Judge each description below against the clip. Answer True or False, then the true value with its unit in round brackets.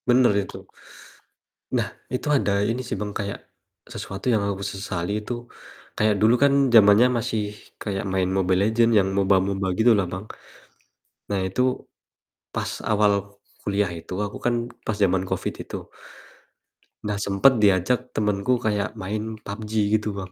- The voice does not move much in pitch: True (2.3 semitones)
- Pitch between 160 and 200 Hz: False (105 Hz)